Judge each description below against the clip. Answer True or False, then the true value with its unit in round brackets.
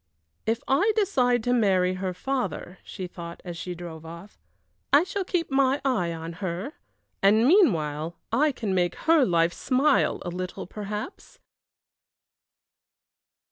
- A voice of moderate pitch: False (200 Hz)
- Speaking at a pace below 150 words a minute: True (140 wpm)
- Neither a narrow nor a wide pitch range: False (7.6 semitones)